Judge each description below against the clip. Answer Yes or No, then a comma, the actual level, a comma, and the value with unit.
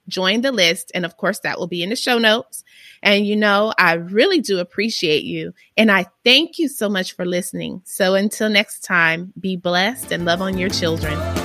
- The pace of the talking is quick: Yes, fast, 210 wpm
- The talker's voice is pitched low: No, high, 190 Hz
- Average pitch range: Yes, average, 3.5 semitones